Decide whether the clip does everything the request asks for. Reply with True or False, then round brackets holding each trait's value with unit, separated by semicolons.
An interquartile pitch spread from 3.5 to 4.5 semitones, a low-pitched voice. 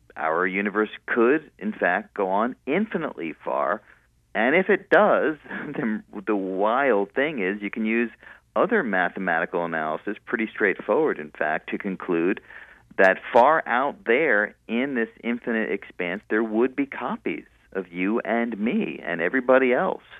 True (3.8 semitones; 110 Hz)